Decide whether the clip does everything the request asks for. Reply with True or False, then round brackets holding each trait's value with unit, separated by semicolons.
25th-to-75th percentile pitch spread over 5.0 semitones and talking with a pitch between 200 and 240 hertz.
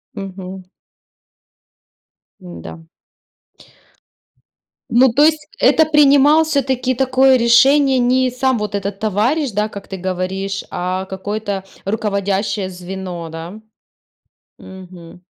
True (5.6 semitones; 205 Hz)